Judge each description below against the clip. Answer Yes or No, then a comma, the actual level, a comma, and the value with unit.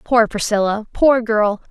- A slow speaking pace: Yes, slow, 105 wpm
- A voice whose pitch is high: Yes, high, 220 Hz